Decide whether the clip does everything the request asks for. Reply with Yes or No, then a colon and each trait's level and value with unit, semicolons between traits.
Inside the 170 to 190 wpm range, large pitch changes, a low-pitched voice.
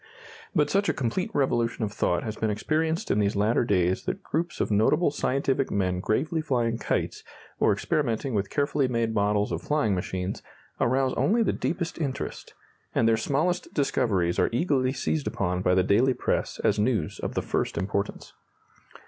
Yes: average, 175 wpm; wide, 6.1 semitones; low, 115 Hz